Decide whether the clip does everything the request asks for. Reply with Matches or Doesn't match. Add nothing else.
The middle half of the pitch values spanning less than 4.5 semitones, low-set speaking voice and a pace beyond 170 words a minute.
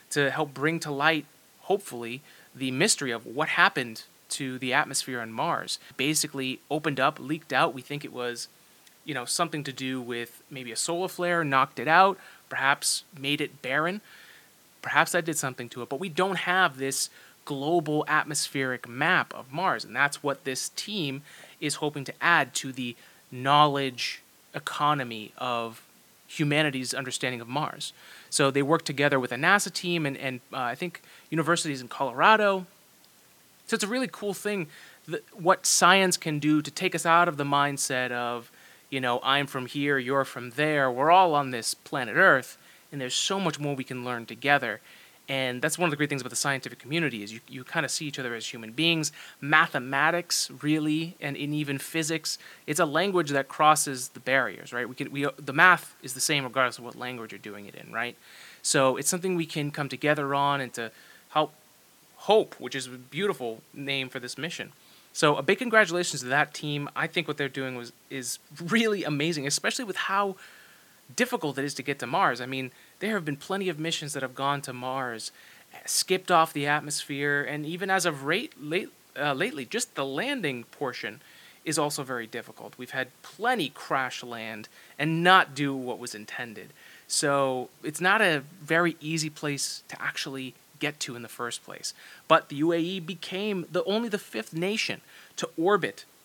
Doesn't match